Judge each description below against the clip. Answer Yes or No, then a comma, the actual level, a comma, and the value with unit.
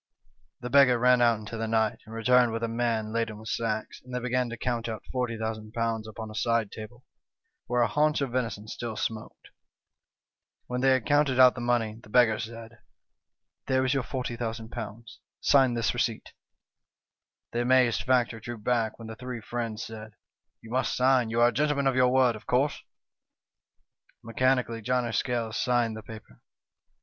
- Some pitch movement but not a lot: No, narrow, 2.0 semitones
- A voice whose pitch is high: No, low, 120 Hz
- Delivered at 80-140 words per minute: No, average, 190 wpm